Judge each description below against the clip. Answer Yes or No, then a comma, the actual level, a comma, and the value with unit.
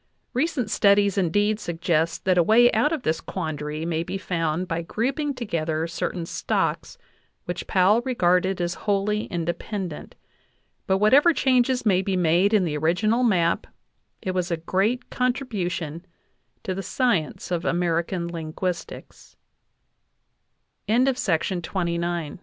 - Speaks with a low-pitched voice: No, medium, 185 Hz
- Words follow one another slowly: Yes, slow, 125 wpm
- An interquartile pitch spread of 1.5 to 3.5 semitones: No, average, 4.3 semitones